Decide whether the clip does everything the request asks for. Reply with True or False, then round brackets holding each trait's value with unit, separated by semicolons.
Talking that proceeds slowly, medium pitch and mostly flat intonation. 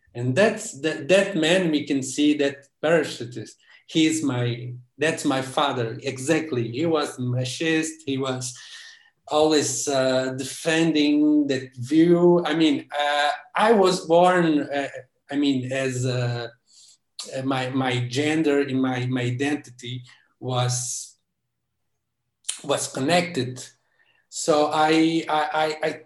False (120 wpm; 145 Hz; 3.7 semitones)